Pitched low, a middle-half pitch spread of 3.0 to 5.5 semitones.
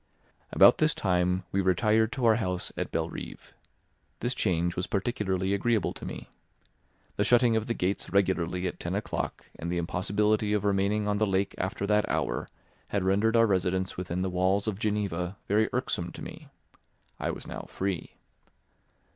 No: low, 100 Hz; narrow, 2.6 semitones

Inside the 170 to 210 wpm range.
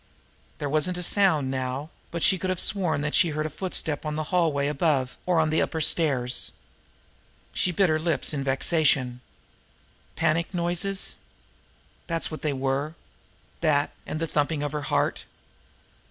No: average, 160 wpm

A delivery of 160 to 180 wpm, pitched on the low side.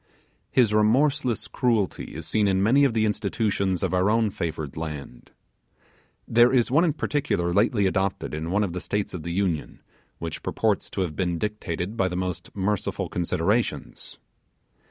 Yes: average, 165 wpm; low, 100 Hz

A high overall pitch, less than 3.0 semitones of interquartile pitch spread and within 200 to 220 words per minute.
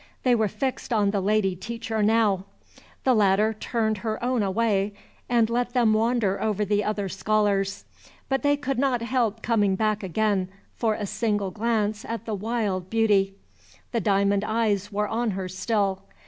No: high, 215 Hz; narrow, 2.5 semitones; average, 165 wpm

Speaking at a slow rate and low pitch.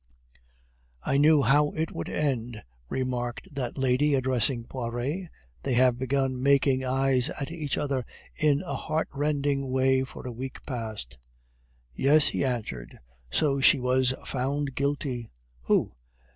Yes: slow, 130 wpm; low, 130 Hz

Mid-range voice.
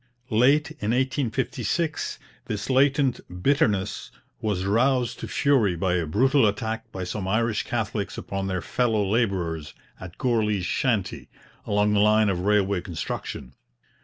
No: low, 105 Hz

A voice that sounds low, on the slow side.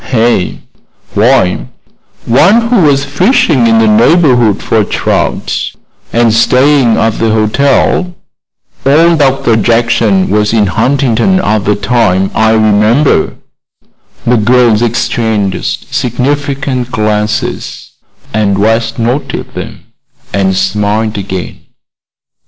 Yes: low, 115 Hz; slow, 105 wpm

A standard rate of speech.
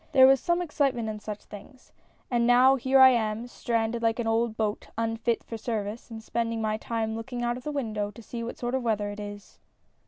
No: fast, 220 wpm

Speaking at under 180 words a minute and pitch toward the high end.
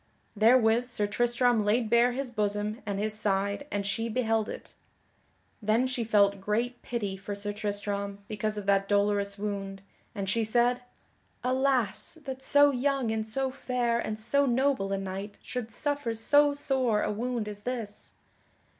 Yes: average, 160 wpm; high, 220 Hz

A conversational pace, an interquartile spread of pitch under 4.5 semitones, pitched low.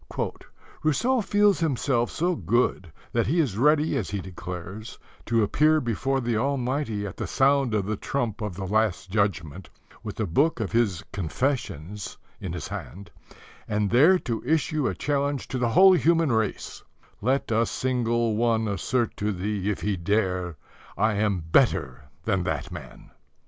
No: average, 160 wpm; wide, 5.6 semitones; low, 110 Hz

